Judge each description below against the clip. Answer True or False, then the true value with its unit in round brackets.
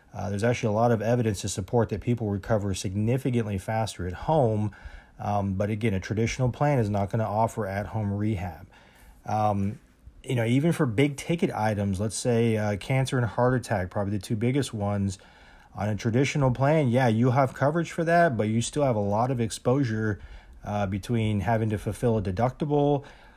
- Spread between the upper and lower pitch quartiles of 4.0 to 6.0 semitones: False (3.5 semitones)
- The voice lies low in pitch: True (110 Hz)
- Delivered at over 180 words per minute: True (195 wpm)